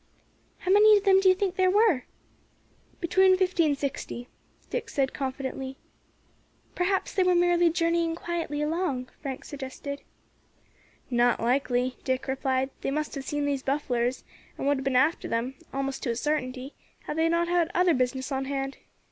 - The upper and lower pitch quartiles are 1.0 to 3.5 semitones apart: No, average, 4.8 semitones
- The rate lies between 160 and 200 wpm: Yes, average, 165 wpm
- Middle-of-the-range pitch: No, very high, 285 Hz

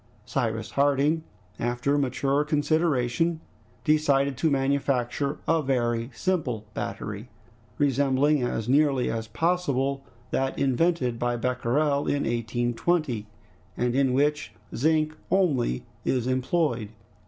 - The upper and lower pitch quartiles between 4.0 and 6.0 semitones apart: No, average, 3.6 semitones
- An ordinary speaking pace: No, slow, 105 wpm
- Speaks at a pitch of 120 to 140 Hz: Yes, low, 135 Hz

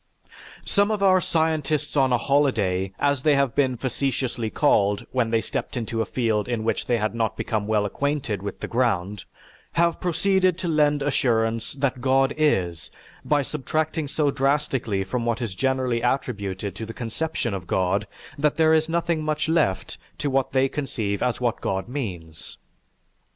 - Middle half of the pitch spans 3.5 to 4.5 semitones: No, average, 5.2 semitones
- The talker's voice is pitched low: Yes, low, 130 Hz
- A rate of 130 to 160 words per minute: No, average, 170 wpm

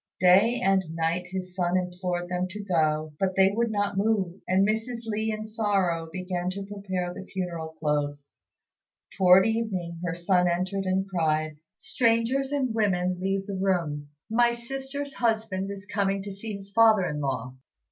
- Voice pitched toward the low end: No, high, 190 Hz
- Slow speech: No, average, 165 wpm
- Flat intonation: No, average, 3.3 semitones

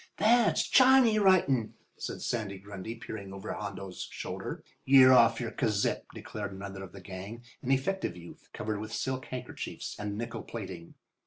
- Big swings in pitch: No, average, 4.8 semitones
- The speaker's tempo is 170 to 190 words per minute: No, average, 155 wpm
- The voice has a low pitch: Yes, low, 110 Hz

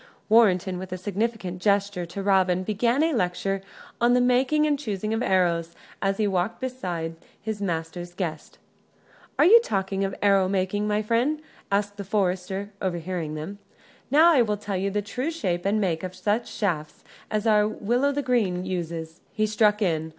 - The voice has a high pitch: Yes, high, 200 Hz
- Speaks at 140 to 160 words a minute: No, average, 170 wpm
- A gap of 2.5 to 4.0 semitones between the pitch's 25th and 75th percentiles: Yes, average, 3.5 semitones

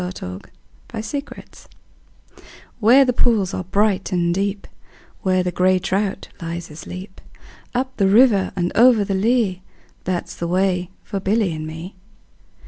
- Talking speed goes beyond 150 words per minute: No, average, 145 wpm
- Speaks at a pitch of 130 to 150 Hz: No, high, 190 Hz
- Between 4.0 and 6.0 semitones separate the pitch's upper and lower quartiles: No, average, 3.2 semitones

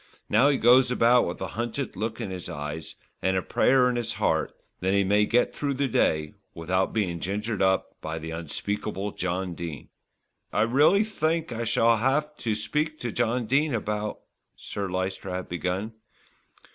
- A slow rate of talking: No, average, 180 wpm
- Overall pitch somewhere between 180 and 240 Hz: No, low, 105 Hz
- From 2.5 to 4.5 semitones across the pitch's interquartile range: No, average, 5.0 semitones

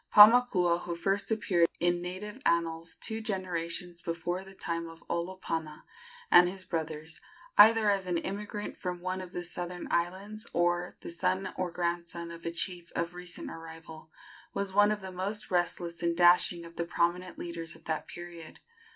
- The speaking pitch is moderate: Yes, medium, 175 Hz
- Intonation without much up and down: Yes, narrow, 2.0 semitones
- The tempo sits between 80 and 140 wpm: No, average, 170 wpm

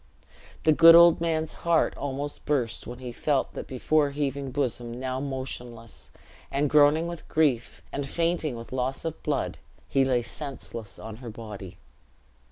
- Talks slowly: No, average, 155 wpm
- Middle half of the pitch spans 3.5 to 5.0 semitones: Yes, average, 3.9 semitones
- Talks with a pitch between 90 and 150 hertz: Yes, low, 135 Hz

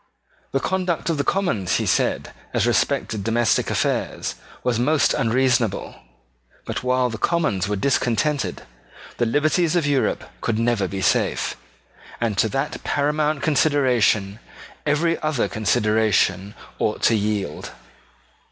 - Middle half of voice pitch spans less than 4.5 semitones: No, wide, 5.6 semitones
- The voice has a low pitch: Yes, low, 120 Hz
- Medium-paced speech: No, slow, 125 wpm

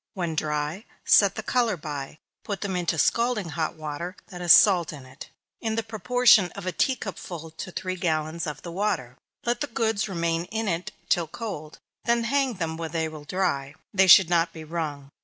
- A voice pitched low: No, medium, 175 Hz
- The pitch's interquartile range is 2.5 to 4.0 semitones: No, average, 5.0 semitones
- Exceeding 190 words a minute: Yes, average, 200 wpm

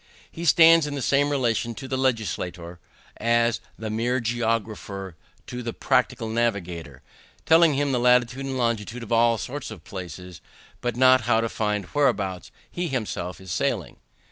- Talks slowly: No, average, 160 wpm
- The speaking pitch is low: Yes, low, 115 Hz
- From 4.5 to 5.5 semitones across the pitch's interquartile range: No, average, 4.0 semitones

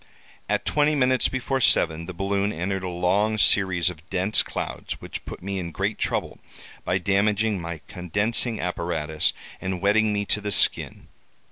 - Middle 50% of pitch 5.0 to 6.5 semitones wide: No, average, 3.1 semitones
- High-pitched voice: No, very low, 95 Hz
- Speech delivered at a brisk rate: No, average, 160 wpm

